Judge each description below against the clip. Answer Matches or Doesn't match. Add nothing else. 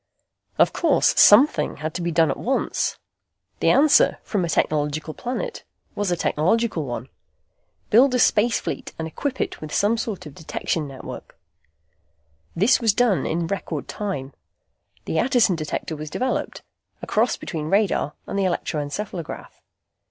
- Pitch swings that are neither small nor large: Doesn't match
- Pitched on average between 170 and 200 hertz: Matches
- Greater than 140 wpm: Matches